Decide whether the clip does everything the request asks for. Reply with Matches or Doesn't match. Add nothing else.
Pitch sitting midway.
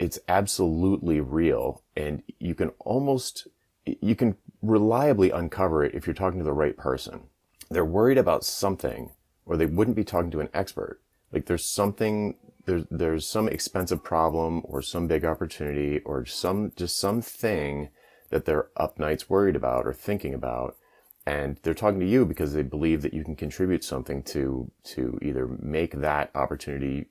Doesn't match